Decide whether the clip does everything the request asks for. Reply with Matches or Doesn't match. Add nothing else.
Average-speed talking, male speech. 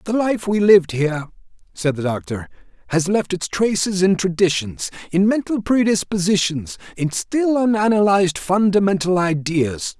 Doesn't match